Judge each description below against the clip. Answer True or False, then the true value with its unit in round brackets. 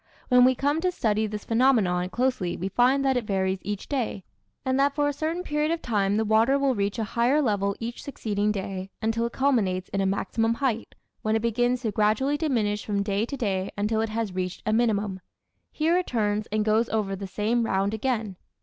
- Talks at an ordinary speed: False (215 wpm)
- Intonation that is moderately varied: True (4.1 semitones)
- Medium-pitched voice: False (220 Hz)